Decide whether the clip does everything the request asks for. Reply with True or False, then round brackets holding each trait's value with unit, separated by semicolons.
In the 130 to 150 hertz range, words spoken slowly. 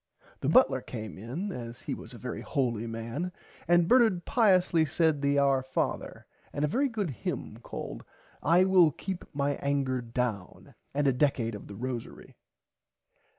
False (140 Hz; 160 wpm)